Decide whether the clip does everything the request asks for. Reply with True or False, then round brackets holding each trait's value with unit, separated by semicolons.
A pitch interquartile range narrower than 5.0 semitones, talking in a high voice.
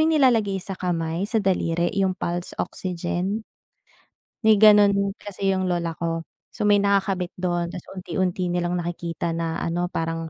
False (2.7 semitones; 180 Hz)